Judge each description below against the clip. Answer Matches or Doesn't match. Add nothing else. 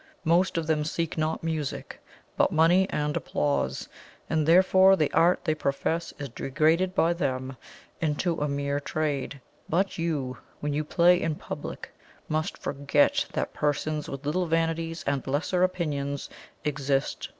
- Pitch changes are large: Doesn't match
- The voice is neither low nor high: Matches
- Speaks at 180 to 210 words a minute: Doesn't match